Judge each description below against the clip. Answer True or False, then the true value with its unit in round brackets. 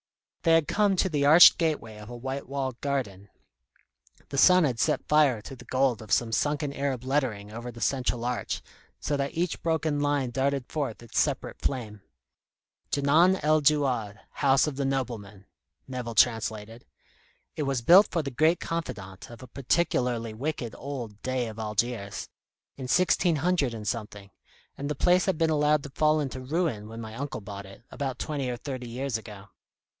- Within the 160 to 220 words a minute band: True (180 wpm)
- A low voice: True (130 Hz)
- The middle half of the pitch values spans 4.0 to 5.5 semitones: True (4.5 semitones)